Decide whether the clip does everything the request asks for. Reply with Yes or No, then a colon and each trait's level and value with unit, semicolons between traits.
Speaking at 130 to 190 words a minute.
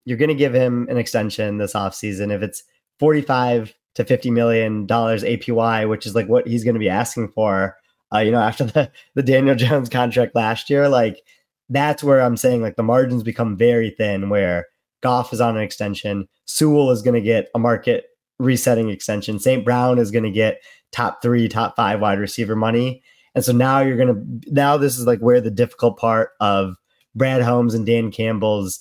No: average, 200 wpm